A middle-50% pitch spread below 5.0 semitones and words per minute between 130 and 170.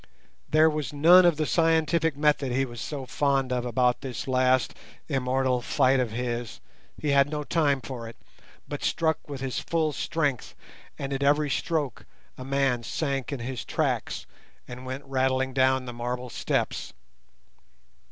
Yes: average, 2.7 semitones; average, 160 wpm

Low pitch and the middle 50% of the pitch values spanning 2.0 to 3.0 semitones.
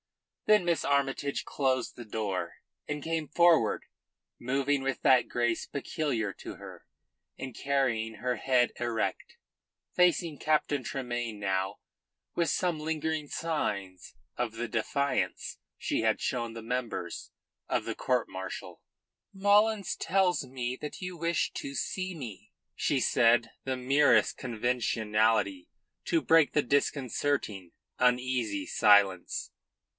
No: low, 130 Hz; average, 5.0 semitones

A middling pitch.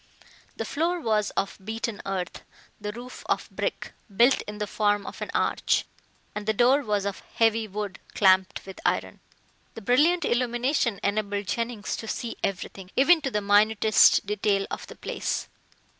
No: high, 215 Hz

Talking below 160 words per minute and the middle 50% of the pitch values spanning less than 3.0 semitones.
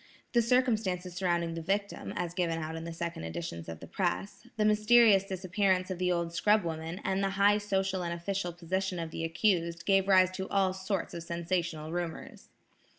No: average, 190 wpm; narrow, 2.6 semitones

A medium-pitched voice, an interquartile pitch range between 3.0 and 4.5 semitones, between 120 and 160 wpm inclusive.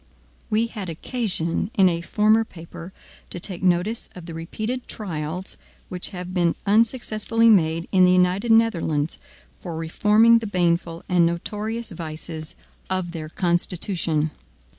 Yes: medium, 180 Hz; average, 4.2 semitones; slow, 135 wpm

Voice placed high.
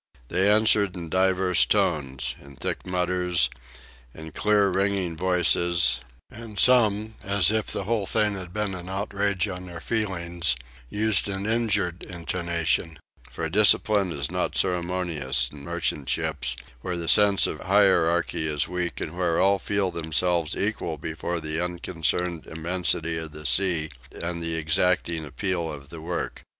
No: very low, 90 Hz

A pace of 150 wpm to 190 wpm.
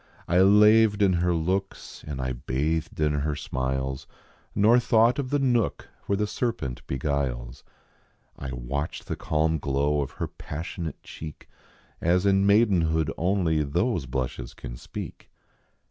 No: average, 140 wpm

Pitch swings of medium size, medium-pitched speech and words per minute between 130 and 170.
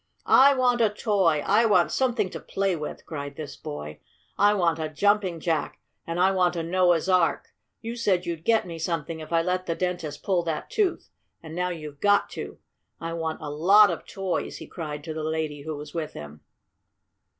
No: average, 3.9 semitones; medium, 170 Hz; average, 200 wpm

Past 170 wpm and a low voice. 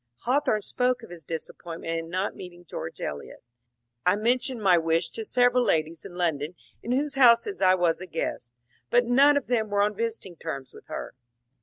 No: average, 190 wpm; high, 190 Hz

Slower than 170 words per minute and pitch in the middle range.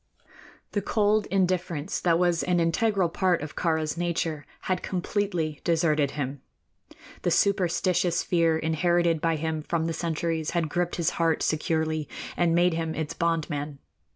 Yes: average, 150 wpm; medium, 165 Hz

